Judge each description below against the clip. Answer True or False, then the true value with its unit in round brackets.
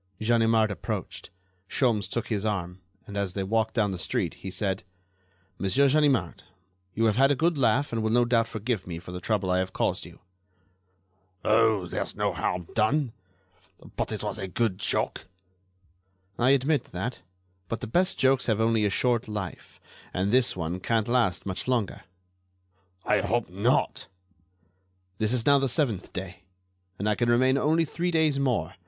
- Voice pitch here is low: True (110 Hz)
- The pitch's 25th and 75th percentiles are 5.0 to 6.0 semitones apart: False (4.6 semitones)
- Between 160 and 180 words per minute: True (170 wpm)